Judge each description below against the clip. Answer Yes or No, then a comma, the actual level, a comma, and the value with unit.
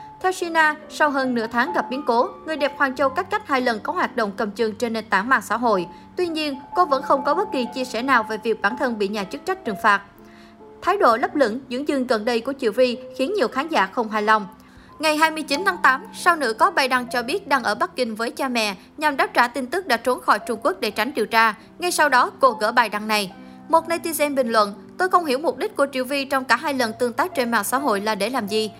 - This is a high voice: Yes, very high, 255 Hz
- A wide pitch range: No, average, 5.0 semitones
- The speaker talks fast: Yes, fast, 280 wpm